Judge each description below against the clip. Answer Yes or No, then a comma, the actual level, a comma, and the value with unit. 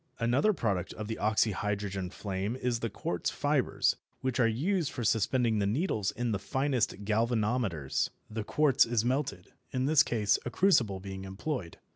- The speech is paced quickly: No, average, 160 wpm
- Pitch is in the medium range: No, low, 110 Hz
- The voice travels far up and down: No, average, 4.1 semitones